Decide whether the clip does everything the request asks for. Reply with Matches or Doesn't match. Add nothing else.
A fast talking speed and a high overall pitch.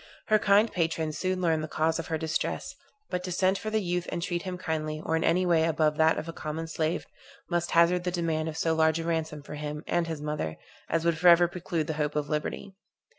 Doesn't match